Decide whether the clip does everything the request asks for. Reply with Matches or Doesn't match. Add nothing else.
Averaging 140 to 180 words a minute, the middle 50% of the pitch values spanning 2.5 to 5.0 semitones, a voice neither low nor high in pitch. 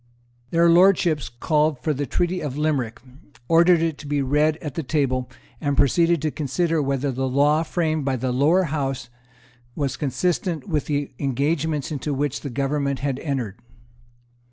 Matches